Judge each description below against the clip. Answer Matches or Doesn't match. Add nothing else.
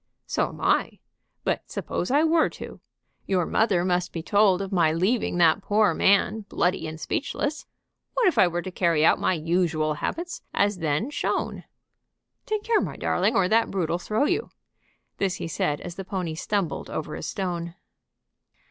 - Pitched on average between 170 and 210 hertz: Matches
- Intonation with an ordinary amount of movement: Matches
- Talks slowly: Doesn't match